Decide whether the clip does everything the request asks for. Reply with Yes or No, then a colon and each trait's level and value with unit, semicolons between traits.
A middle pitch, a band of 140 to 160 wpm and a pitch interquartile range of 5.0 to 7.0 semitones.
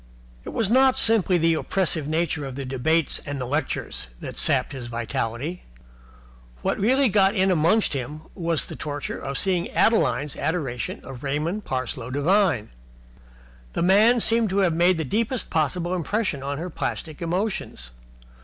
Yes: medium, 165 Hz; average, 155 wpm; wide, 5.6 semitones